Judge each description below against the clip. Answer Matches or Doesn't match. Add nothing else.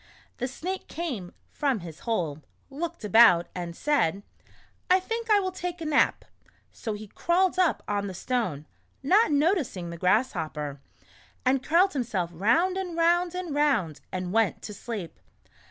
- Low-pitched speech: Doesn't match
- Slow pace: Doesn't match